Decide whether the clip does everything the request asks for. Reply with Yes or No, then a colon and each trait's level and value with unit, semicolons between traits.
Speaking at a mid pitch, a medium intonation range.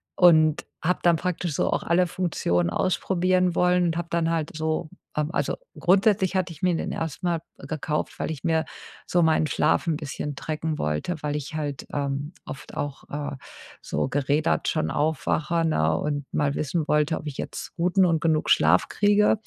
Yes: medium, 160 Hz; average, 3.0 semitones